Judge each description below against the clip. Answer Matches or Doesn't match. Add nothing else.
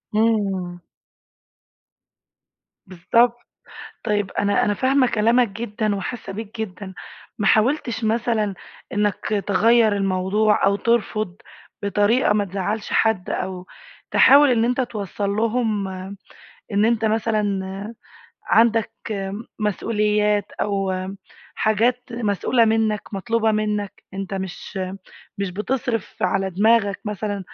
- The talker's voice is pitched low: Doesn't match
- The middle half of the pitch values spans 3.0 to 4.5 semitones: Doesn't match